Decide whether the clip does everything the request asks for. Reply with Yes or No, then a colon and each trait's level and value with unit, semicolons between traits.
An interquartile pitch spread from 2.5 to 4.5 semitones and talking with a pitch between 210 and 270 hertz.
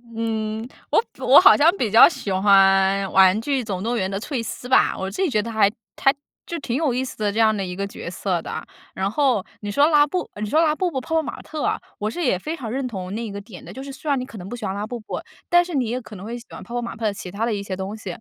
No: average, 5.2 semitones; high, 225 Hz